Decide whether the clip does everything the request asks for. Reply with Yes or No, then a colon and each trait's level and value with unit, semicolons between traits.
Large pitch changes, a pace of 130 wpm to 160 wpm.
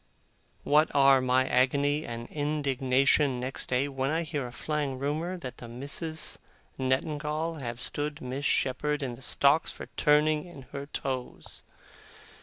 No: narrow, 2.6 semitones; average, 145 wpm